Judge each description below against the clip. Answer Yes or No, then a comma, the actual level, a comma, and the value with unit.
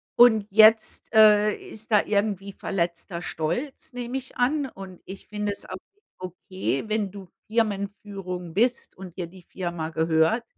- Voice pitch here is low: No, high, 200 Hz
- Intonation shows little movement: No, average, 3.3 semitones